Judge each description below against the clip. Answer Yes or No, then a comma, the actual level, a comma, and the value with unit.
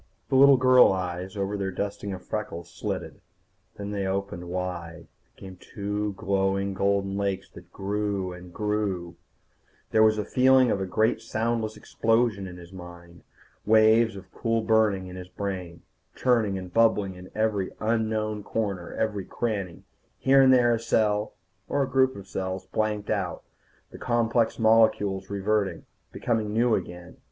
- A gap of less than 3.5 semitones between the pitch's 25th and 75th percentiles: Yes, average, 2.8 semitones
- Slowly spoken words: No, average, 155 wpm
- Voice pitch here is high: No, low, 100 Hz